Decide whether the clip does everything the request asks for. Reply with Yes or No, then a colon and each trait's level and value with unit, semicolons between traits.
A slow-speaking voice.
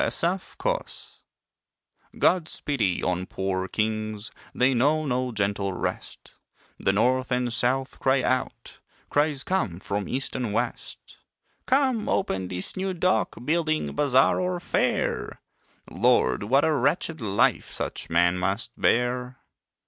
Yes: slow, 125 wpm